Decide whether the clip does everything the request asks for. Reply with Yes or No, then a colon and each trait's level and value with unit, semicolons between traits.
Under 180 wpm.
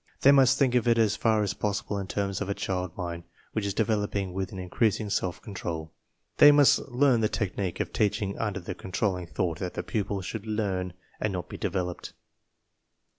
No: average, 195 wpm